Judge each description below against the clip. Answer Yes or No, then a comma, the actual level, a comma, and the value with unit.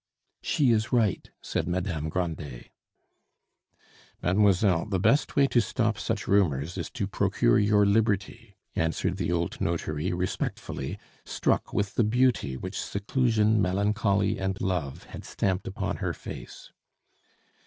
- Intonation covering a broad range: No, average, 3.7 semitones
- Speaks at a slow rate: Yes, slow, 130 wpm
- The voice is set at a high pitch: No, low, 100 Hz